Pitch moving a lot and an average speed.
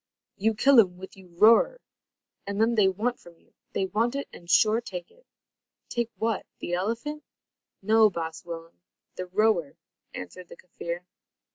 No: average, 4.4 semitones; average, 160 wpm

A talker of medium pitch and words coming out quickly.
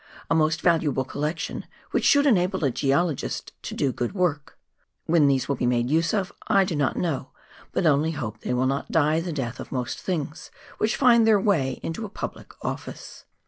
No: medium, 155 Hz; average, 195 wpm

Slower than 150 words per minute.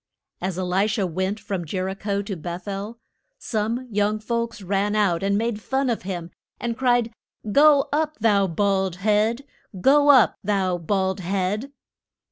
No: average, 165 wpm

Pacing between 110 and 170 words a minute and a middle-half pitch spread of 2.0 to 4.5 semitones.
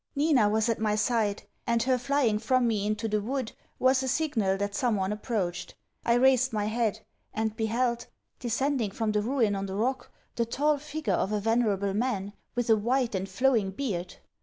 No: average, 190 wpm; average, 3.6 semitones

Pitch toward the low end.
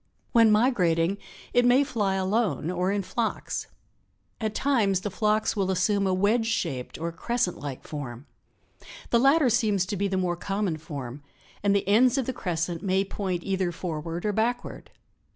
No: high, 195 Hz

